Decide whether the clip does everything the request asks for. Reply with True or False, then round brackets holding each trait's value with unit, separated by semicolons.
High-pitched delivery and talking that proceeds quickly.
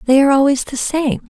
True (275 Hz; 220 wpm)